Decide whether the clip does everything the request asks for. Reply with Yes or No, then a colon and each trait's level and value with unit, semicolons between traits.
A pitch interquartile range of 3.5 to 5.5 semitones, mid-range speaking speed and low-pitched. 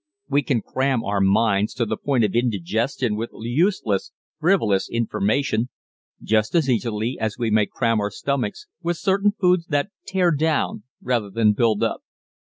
Yes: average, 5.1 semitones; average, 160 wpm; low, 115 Hz